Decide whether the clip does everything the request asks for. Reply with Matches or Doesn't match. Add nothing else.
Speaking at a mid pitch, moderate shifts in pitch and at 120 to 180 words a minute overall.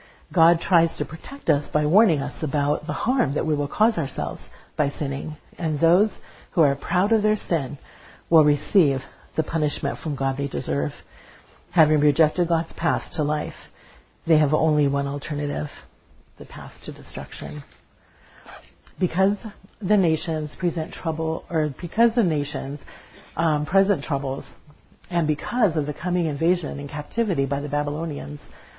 Matches